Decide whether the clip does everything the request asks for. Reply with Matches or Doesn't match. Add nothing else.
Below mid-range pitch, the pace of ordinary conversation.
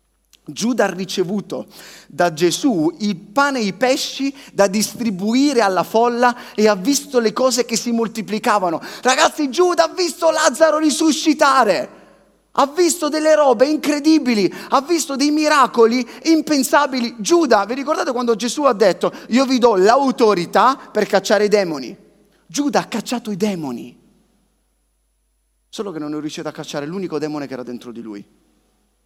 Doesn't match